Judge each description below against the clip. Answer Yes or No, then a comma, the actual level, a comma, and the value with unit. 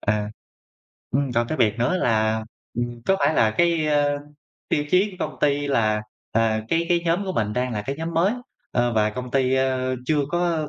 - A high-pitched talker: No, low, 130 Hz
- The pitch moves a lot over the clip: Yes, wide, 6.1 semitones